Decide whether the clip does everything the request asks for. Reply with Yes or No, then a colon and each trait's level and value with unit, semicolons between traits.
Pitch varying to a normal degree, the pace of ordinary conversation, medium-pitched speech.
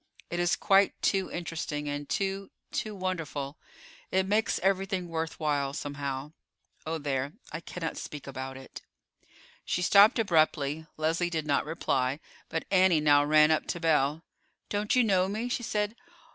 Yes: average, 4.7 semitones; average, 150 wpm; medium, 165 Hz